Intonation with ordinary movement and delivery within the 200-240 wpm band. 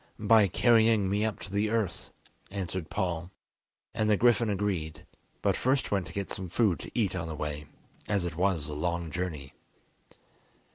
No: average, 4.2 semitones; average, 175 wpm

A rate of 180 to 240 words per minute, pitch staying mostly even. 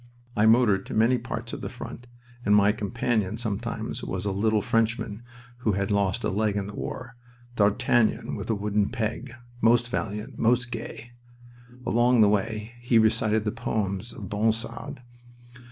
No: average, 160 wpm; narrow, 2.3 semitones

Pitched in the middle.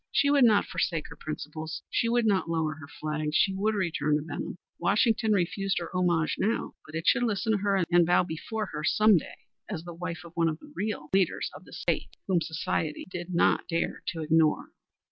Yes: medium, 175 Hz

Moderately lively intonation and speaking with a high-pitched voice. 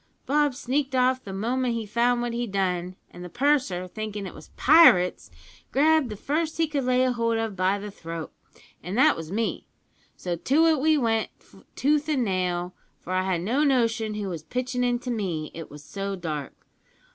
No: wide, 5.9 semitones; high, 225 Hz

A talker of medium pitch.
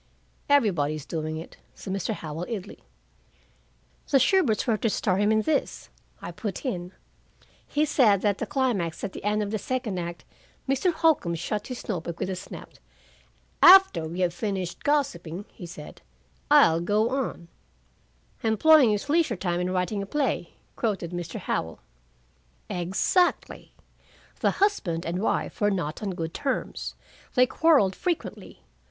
No: high, 200 Hz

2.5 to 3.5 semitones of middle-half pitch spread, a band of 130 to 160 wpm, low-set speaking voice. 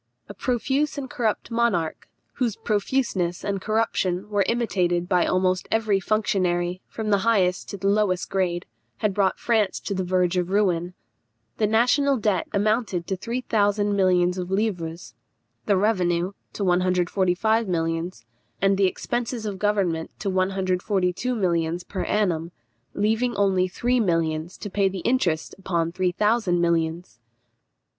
No: average, 3.2 semitones; average, 140 wpm; high, 190 Hz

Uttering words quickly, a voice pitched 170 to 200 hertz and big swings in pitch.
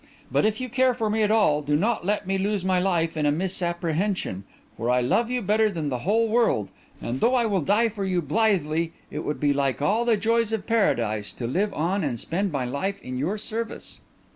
Yes: fast, 225 wpm; high, 190 Hz; wide, 6.6 semitones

